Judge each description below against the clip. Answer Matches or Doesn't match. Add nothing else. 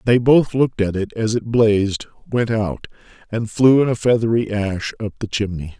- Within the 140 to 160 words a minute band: Doesn't match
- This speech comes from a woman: Doesn't match